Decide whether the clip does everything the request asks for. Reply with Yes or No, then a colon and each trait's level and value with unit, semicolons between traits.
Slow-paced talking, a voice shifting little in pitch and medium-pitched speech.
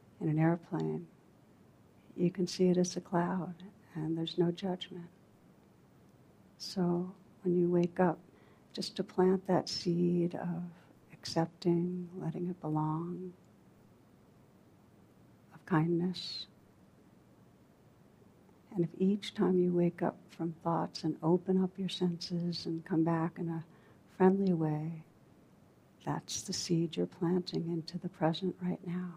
Yes: slow, 130 wpm; narrow, 1.7 semitones; medium, 175 Hz